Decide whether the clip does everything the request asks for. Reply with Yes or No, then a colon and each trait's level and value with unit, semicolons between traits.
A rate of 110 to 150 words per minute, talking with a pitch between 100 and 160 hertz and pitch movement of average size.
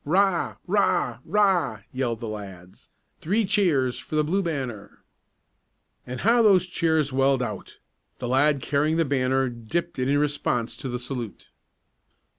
No: slow, 135 wpm; medium, 140 Hz; wide, 5.7 semitones